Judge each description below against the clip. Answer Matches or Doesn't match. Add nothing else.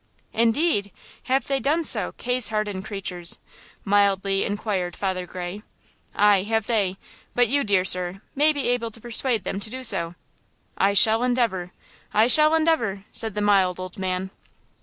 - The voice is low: Doesn't match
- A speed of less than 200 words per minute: Matches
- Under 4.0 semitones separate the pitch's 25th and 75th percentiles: Doesn't match